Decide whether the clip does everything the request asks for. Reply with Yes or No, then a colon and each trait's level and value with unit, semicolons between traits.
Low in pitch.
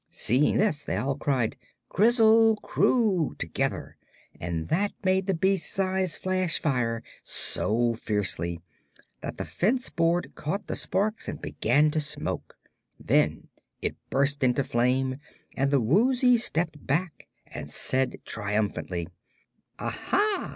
No: medium, 150 Hz